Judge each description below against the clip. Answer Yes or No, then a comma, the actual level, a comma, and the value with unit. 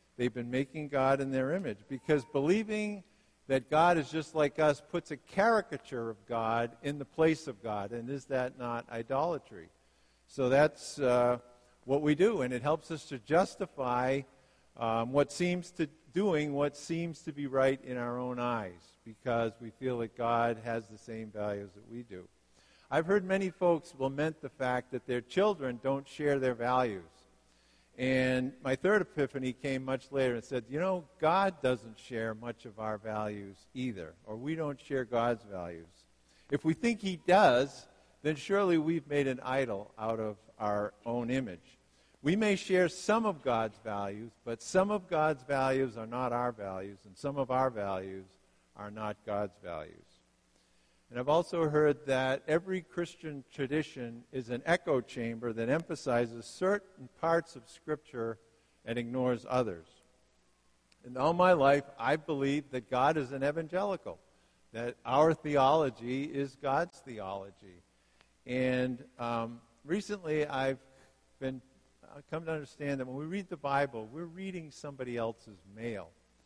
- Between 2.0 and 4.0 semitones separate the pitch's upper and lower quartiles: No, average, 4.9 semitones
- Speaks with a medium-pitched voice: No, low, 130 Hz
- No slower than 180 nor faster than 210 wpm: No, average, 160 wpm